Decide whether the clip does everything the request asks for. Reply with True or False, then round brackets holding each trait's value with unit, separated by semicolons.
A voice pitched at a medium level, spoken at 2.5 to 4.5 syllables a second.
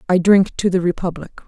False (180 Hz; 5.5 syllables/s)